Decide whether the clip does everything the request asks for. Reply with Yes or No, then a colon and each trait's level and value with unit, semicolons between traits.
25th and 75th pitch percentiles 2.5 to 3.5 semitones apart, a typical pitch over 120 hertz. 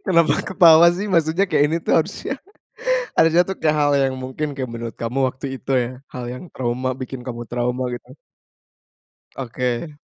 No: average, 4.6 semitones; low, 135 Hz